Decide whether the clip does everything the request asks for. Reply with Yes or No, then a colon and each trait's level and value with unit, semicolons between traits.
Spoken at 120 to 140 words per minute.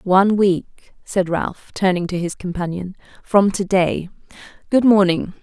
Yes: slow, 135 wpm